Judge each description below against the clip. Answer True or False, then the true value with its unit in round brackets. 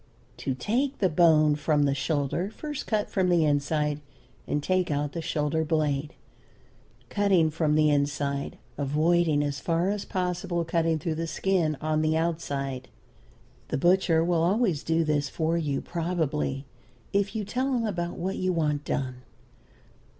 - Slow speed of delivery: False (155 wpm)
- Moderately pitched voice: True (160 Hz)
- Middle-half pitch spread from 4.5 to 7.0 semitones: False (3.3 semitones)